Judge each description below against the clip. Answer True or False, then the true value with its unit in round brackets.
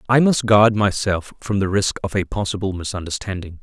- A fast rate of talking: False (180 wpm)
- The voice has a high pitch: False (100 Hz)